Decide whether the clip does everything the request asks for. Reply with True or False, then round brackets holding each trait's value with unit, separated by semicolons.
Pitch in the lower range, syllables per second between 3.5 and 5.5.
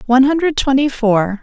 False (260 Hz; 5.4 syllables/s)